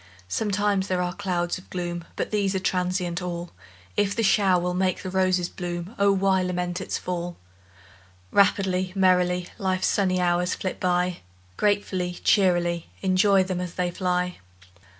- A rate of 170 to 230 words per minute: No, average, 150 wpm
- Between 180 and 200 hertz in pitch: Yes, medium, 185 Hz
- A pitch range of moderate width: No, narrow, 1.3 semitones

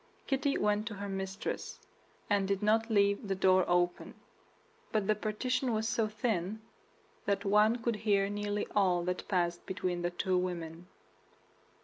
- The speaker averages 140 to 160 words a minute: Yes, average, 150 wpm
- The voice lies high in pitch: Yes, high, 200 Hz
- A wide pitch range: No, average, 2.7 semitones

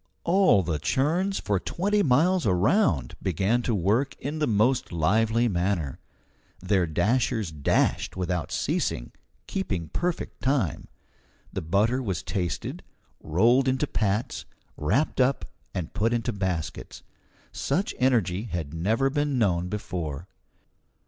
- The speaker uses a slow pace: Yes, slow, 120 wpm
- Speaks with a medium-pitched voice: No, low, 105 Hz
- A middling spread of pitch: No, wide, 6.9 semitones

